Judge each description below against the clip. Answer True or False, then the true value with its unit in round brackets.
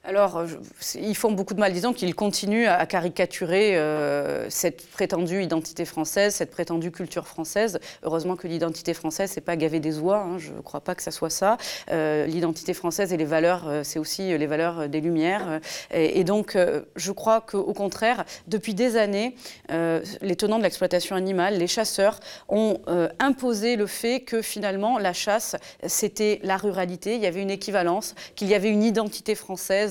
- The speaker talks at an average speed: True (185 wpm)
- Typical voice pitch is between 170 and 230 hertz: True (190 Hz)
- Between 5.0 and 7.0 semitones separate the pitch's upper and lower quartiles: False (3.8 semitones)